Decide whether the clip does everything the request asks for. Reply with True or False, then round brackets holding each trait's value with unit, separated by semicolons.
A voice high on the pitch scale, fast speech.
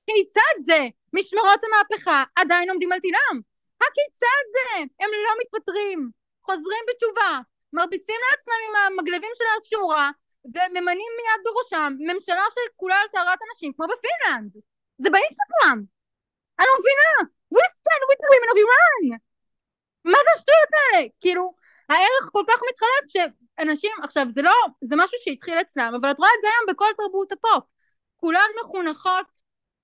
False (370 Hz; 140 wpm)